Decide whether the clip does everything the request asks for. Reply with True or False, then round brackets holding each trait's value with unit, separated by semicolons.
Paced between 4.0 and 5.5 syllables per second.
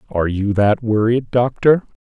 True (4.9 syllables/s)